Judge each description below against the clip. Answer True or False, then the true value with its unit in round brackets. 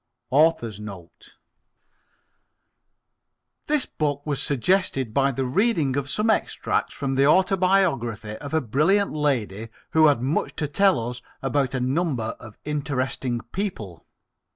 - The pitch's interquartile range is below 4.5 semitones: False (4.8 semitones)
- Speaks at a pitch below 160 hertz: True (140 Hz)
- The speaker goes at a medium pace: False (130 wpm)